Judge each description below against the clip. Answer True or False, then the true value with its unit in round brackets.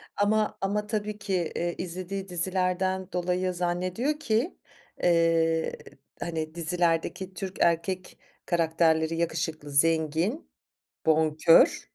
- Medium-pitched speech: True (175 Hz)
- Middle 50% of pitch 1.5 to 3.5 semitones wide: True (2.6 semitones)